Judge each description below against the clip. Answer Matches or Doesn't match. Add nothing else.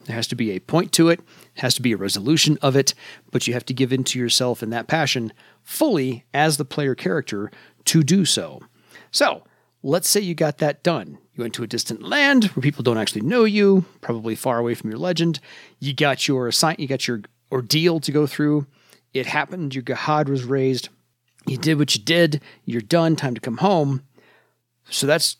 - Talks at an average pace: Doesn't match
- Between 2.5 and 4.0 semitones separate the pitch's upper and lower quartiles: Doesn't match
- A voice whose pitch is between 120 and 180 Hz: Matches